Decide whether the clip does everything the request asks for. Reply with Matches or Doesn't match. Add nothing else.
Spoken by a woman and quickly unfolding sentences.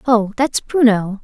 Doesn't match